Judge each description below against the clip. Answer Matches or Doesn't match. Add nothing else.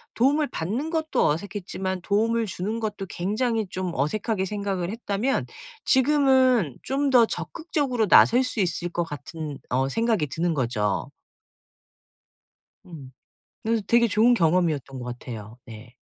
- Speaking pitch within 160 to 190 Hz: Doesn't match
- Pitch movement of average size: Doesn't match